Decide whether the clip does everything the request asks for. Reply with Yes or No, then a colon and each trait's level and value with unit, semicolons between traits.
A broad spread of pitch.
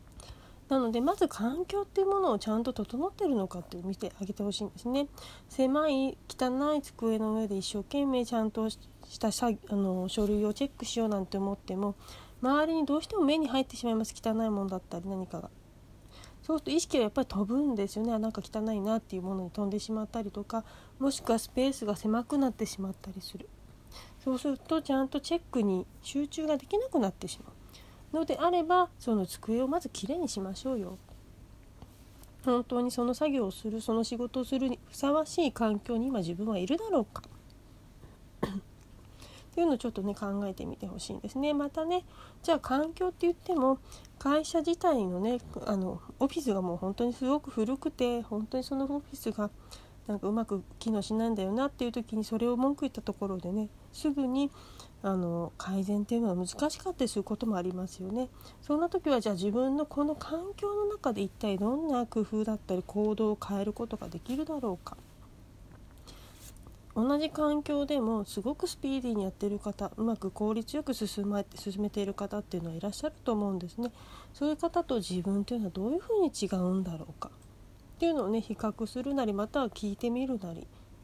Yes: wide, 5.7 semitones